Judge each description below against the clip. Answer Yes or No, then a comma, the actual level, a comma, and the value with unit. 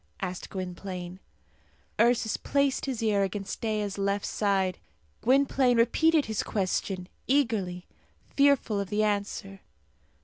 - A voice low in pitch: No, high, 205 Hz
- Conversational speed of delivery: No, slow, 110 wpm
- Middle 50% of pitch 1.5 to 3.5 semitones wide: No, average, 4.0 semitones